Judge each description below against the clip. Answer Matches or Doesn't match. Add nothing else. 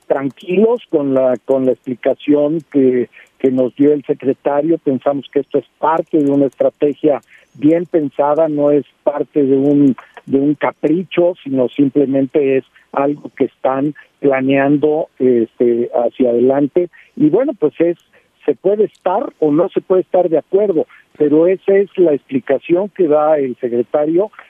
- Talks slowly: Doesn't match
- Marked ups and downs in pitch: Doesn't match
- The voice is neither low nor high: Matches